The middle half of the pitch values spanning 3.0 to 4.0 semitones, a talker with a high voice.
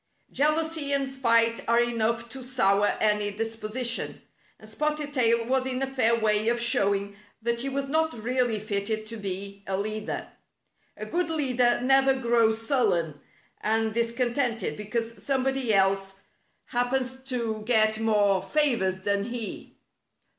Yes: average, 3.5 semitones; high, 230 Hz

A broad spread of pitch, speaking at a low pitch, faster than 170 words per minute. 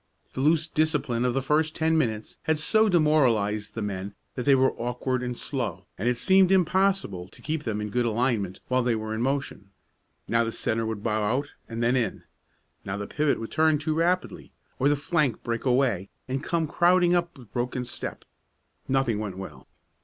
Yes: wide, 5.7 semitones; low, 125 Hz; average, 195 wpm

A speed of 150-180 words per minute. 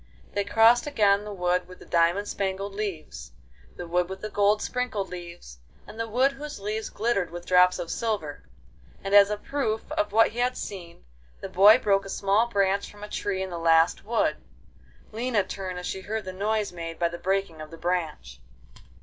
No: average, 195 wpm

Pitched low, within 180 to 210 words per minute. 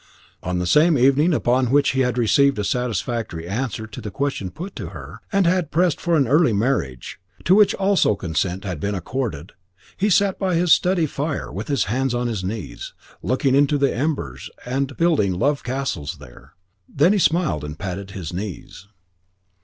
Yes: low, 130 Hz; average, 185 wpm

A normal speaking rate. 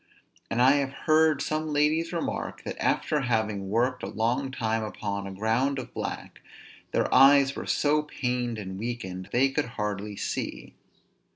Yes: average, 160 wpm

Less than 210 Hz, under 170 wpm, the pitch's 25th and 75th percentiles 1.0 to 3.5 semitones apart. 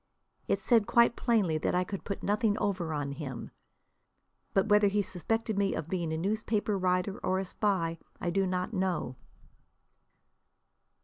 Yes: high, 190 Hz; average, 160 wpm; average, 3.2 semitones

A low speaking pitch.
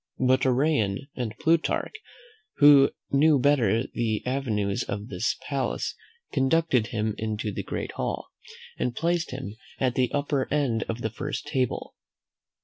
Yes: low, 130 Hz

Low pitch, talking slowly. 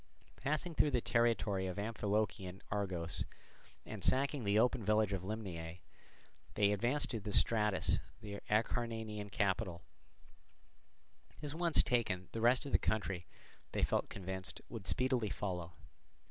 Yes: low, 105 Hz; slow, 130 wpm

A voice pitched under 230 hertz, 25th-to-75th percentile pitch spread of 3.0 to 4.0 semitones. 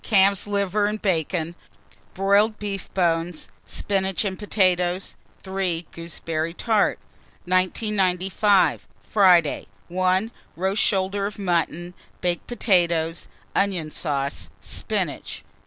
No: medium, 185 Hz; narrow, 2.6 semitones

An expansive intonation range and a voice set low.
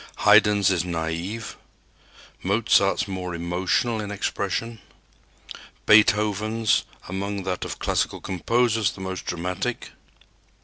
No: average, 2.8 semitones; low, 100 Hz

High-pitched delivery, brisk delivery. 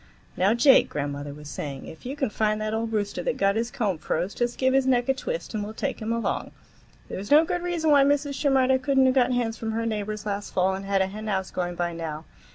Yes: high, 220 Hz; fast, 250 wpm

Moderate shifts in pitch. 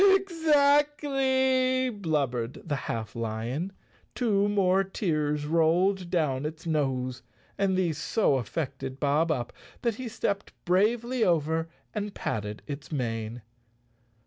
No: wide, 8.0 semitones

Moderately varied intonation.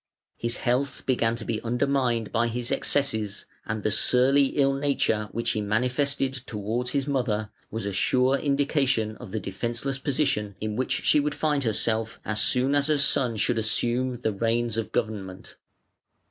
Yes: average, 3.9 semitones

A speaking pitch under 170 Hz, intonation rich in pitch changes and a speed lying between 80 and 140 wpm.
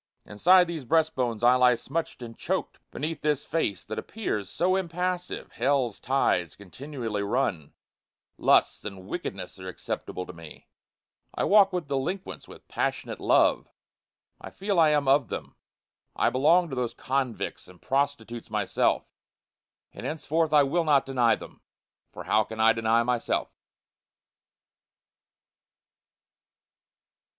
Yes: low, 135 Hz; wide, 6.2 semitones; slow, 135 wpm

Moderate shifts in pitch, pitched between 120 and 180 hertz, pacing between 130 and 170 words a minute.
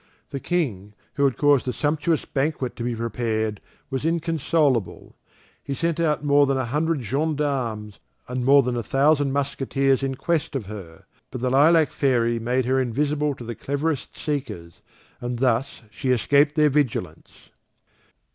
Yes: average, 3.7 semitones; low, 135 Hz; average, 155 wpm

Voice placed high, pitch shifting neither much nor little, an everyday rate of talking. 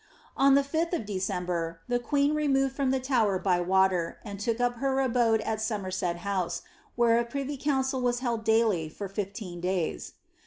No: high, 225 Hz; wide, 5.8 semitones; average, 185 wpm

